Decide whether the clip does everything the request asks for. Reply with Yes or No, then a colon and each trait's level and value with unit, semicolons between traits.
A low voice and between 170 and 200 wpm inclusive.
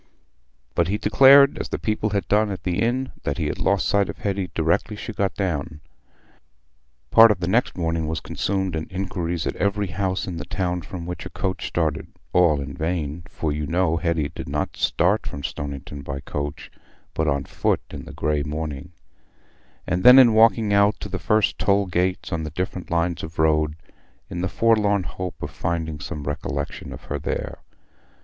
Yes: very low, 90 Hz; average, 185 wpm